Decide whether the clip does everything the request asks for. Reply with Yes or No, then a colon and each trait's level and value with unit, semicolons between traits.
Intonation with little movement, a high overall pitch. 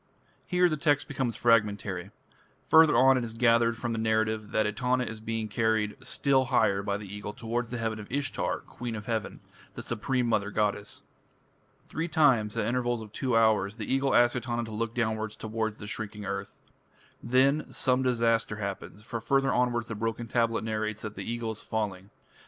No: narrow, 2.3 semitones; low, 115 Hz